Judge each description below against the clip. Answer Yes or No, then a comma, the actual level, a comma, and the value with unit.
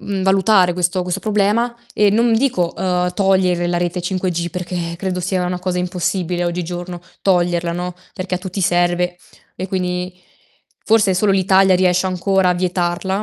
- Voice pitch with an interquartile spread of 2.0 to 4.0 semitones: No, narrow, 1.4 semitones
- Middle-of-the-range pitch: Yes, medium, 180 Hz